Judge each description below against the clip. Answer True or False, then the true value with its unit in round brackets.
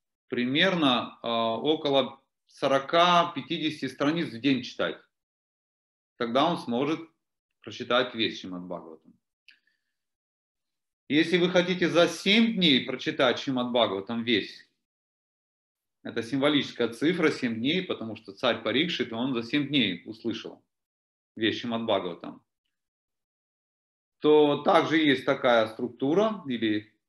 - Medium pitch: False (130 Hz)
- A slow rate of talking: True (105 wpm)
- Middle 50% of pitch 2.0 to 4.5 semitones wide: False (5.4 semitones)